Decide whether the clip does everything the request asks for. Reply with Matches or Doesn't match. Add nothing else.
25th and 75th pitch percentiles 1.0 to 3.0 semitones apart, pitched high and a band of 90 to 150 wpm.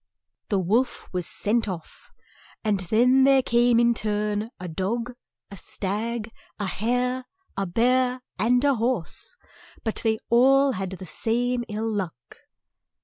Doesn't match